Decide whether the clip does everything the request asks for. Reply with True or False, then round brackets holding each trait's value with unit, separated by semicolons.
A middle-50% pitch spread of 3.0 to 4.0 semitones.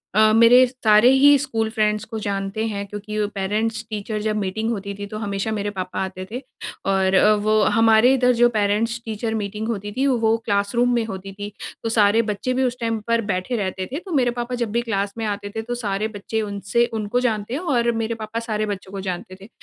False (2.5 semitones)